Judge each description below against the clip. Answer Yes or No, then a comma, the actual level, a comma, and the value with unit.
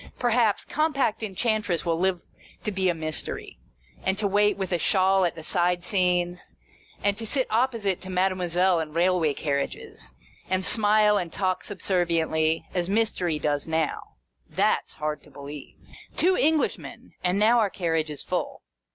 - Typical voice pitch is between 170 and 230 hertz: Yes, medium, 185 Hz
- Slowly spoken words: No, average, 160 wpm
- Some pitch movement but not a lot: Yes, average, 4.0 semitones